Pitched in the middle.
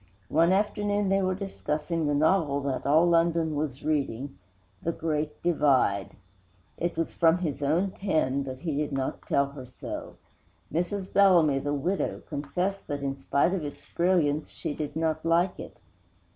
Yes: medium, 155 Hz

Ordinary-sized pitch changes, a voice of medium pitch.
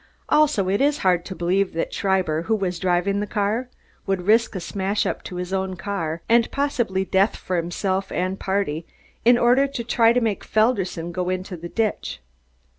No: average, 3.6 semitones; high, 195 Hz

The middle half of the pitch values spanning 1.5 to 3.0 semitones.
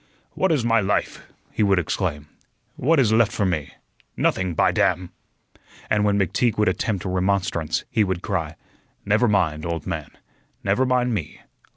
No: average, 4.1 semitones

